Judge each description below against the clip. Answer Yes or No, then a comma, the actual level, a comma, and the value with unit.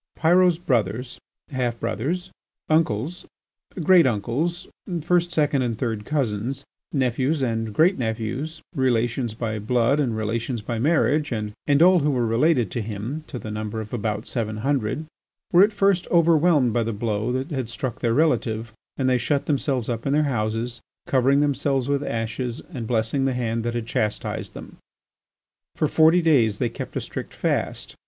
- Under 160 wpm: No, average, 165 wpm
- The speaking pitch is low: Yes, low, 125 Hz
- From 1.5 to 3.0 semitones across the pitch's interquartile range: No, average, 4.8 semitones